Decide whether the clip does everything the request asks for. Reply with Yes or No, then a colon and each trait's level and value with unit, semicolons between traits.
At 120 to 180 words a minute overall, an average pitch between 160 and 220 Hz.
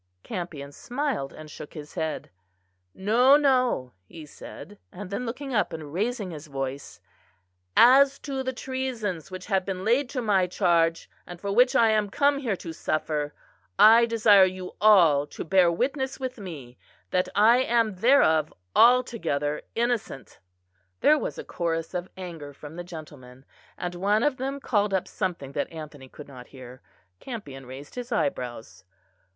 Yes: average, 160 wpm; medium, 185 Hz